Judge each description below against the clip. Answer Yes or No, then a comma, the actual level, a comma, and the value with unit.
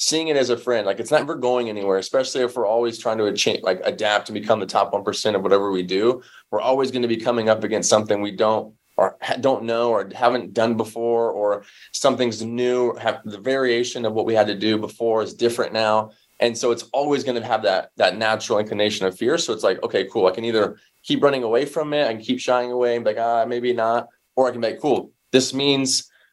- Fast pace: Yes, fast, 245 wpm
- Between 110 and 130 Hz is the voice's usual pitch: Yes, low, 115 Hz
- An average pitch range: No, narrow, 2.3 semitones